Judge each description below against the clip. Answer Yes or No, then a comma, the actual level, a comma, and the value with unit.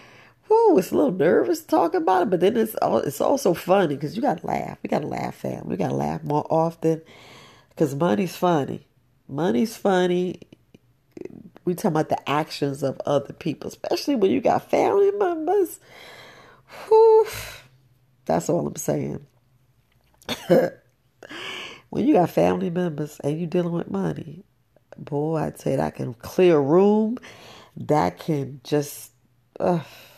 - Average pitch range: No, wide, 6.0 semitones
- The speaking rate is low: No, average, 145 wpm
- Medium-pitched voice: Yes, medium, 165 Hz